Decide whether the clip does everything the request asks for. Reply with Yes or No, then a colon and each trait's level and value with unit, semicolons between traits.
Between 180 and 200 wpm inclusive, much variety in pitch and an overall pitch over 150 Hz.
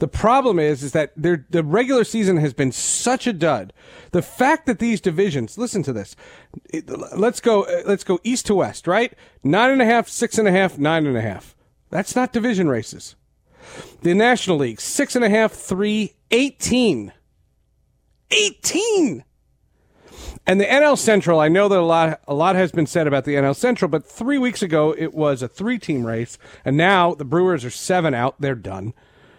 Yes: average, 195 wpm; wide, 7.9 semitones; medium, 185 Hz